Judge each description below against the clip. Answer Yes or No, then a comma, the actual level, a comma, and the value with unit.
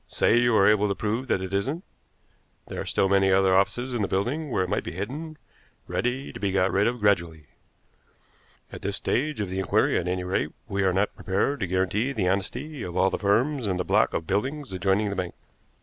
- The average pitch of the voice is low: Yes, low, 100 Hz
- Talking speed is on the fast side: Yes, fast, 225 wpm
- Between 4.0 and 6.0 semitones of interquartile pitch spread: Yes, average, 4.5 semitones